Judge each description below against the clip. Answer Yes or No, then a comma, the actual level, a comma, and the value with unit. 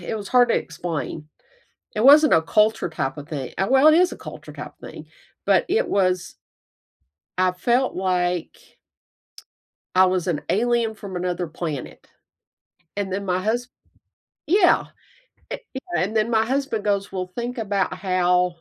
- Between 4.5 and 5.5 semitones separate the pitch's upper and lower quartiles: Yes, average, 4.9 semitones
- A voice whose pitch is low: No, high, 195 Hz